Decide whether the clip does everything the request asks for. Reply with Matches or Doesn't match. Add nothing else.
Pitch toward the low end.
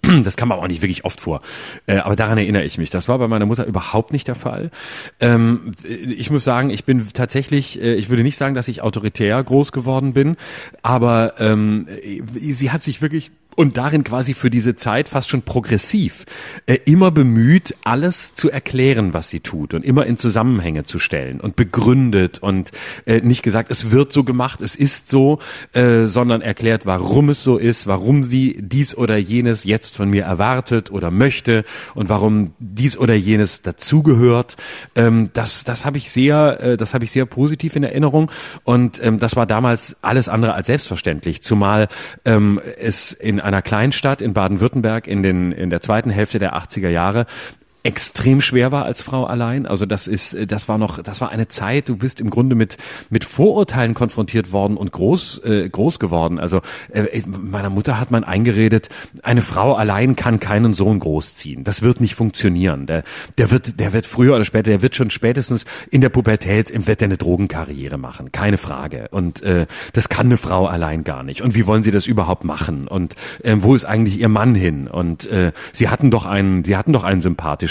Matches